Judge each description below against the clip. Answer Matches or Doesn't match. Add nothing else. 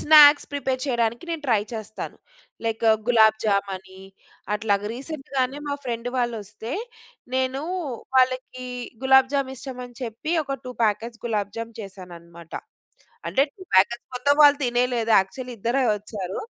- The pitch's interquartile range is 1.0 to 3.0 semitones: Doesn't match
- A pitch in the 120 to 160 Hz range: Doesn't match